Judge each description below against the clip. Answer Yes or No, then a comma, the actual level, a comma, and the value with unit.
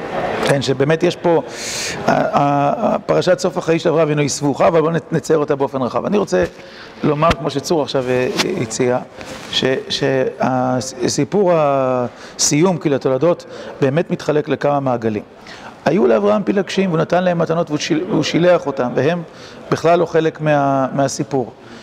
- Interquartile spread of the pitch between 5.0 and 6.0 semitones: No, average, 3.7 semitones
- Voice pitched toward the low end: No, medium, 145 Hz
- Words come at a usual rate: Yes, average, 130 wpm